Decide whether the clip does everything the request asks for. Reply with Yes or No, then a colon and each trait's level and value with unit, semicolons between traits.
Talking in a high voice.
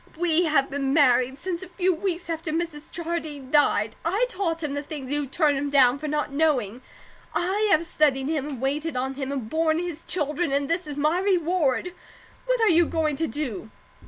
Yes: very high, 305 Hz